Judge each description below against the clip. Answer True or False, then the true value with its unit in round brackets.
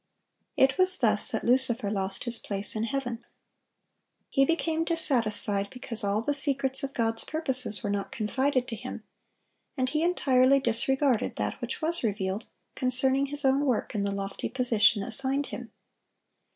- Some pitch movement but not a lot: True (4.2 semitones)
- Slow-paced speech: False (155 wpm)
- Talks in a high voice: True (255 Hz)